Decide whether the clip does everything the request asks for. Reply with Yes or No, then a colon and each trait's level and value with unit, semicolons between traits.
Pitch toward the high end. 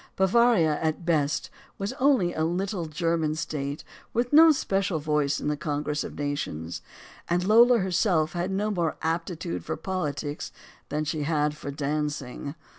No: medium, 160 Hz